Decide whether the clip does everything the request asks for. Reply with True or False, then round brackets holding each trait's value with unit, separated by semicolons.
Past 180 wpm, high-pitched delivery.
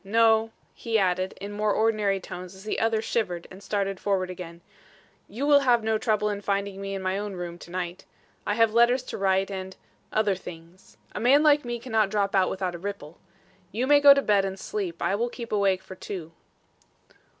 True (205 wpm; 200 Hz)